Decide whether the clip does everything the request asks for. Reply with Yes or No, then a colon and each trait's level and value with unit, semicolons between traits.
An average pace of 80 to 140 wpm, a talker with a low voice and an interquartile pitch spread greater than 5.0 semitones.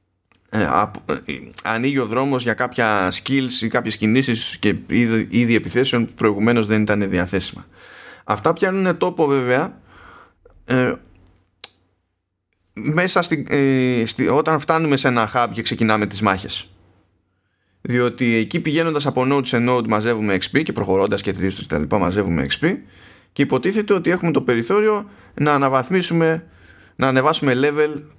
Yes: average, 135 wpm; low, 120 Hz; wide, 5.5 semitones